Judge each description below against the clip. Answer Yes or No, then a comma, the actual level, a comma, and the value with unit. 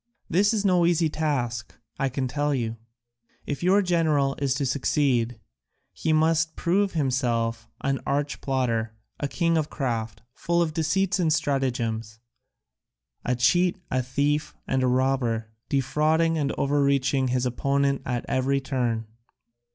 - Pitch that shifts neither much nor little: Yes, average, 4.0 semitones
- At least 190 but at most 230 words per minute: No, average, 140 wpm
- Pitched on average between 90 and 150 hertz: Yes, medium, 140 Hz